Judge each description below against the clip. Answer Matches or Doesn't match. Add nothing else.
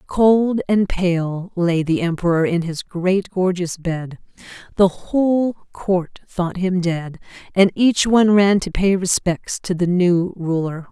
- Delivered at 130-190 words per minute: Matches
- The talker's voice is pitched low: Doesn't match